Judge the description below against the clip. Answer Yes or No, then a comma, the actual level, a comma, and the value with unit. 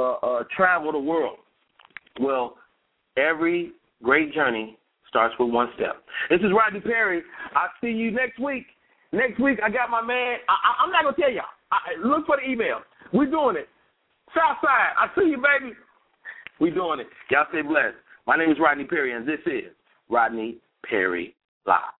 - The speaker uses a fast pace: No, average, 185 wpm